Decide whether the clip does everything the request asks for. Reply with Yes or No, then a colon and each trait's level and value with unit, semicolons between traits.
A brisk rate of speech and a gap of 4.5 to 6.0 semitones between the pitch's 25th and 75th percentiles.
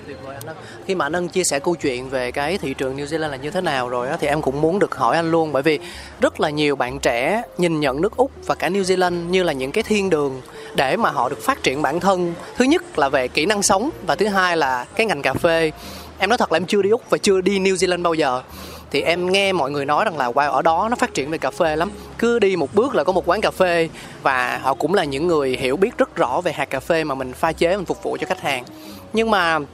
Yes: fast, 280 wpm; wide, 5.5 semitones